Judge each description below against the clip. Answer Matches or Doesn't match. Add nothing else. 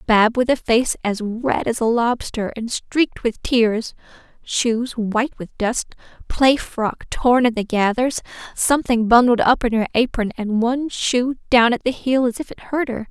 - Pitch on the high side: Matches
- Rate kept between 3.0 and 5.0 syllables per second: Matches